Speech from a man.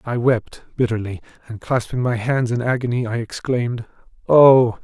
Yes: male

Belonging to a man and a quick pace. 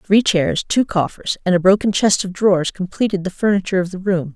No: female; fast, 220 wpm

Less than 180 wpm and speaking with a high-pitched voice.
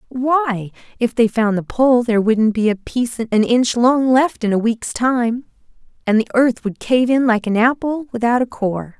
No: fast, 205 wpm; high, 235 Hz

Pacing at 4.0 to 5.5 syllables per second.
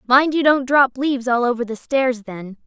Yes: 4.9 syllables/s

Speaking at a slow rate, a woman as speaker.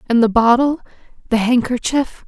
Yes: slow, 105 wpm; female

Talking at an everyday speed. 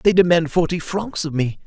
No: fast, 215 wpm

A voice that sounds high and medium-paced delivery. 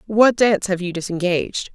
Yes: high, 195 Hz; average, 170 wpm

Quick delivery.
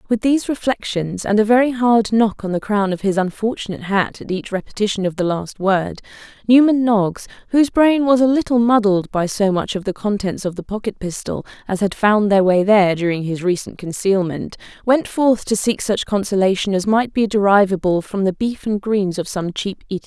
Yes: fast, 210 wpm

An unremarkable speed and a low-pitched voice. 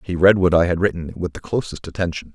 No: fast, 255 wpm; very low, 90 Hz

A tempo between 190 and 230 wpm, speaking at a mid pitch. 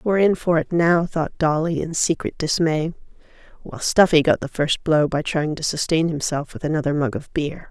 Yes: average, 200 wpm; medium, 155 Hz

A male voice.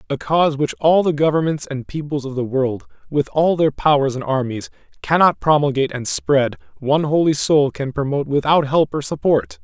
Yes: male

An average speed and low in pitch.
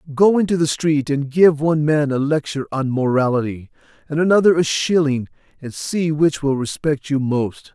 No: average, 180 wpm; medium, 145 Hz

